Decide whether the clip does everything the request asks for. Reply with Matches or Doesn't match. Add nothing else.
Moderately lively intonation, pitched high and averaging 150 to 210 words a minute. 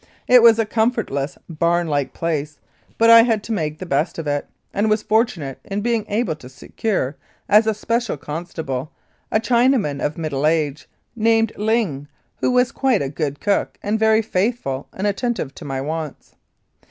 Doesn't match